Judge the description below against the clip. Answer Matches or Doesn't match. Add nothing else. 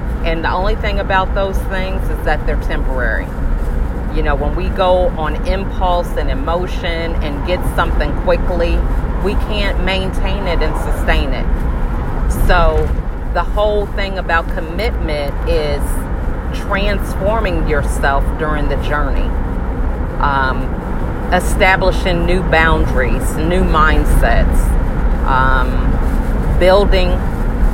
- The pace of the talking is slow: Matches